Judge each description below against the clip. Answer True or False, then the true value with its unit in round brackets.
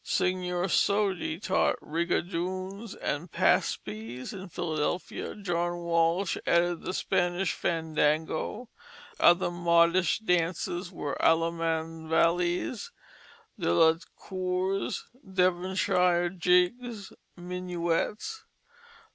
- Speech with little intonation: True (1.9 semitones)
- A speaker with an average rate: False (80 wpm)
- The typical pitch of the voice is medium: True (175 Hz)